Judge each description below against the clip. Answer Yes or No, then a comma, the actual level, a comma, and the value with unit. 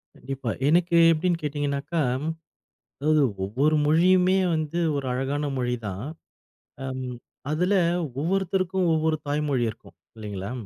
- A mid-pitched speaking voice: Yes, medium, 150 Hz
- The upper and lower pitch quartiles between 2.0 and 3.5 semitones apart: No, average, 4.3 semitones